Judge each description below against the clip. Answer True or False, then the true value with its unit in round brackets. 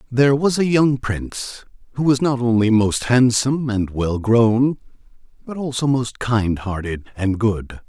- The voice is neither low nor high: False (120 Hz)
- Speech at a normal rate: True (160 wpm)